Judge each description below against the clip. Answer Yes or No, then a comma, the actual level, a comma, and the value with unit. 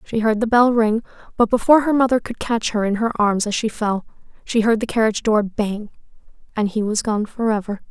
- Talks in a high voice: Yes, high, 220 Hz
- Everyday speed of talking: No, fast, 220 wpm